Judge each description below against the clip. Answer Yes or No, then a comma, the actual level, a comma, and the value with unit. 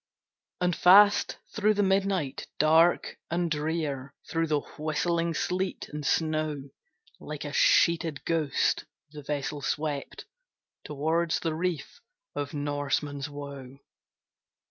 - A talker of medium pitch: Yes, medium, 155 Hz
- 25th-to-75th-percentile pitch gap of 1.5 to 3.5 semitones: Yes, average, 2.8 semitones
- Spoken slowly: Yes, slow, 110 wpm